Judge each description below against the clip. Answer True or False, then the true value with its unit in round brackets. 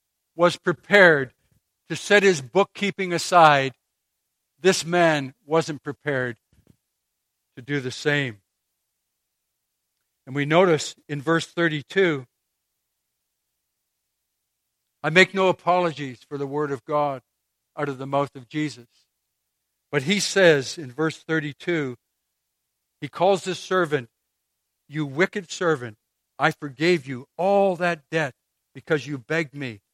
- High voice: False (140 Hz)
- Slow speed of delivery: True (120 wpm)